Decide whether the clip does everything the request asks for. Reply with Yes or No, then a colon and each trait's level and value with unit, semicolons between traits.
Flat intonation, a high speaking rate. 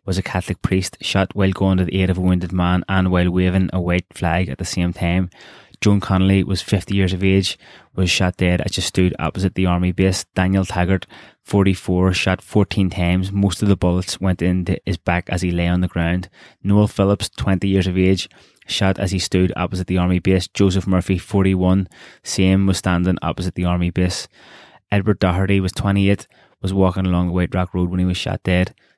Yes: narrow, 1.1 semitones; fast, 210 wpm